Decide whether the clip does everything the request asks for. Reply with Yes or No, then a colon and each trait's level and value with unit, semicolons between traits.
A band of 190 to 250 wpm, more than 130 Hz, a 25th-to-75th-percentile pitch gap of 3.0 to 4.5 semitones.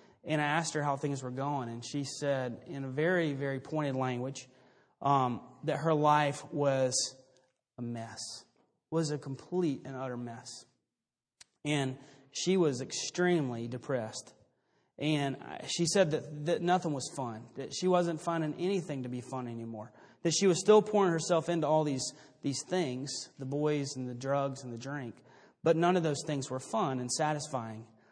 No: average, 175 wpm; medium, 140 Hz; average, 3.3 semitones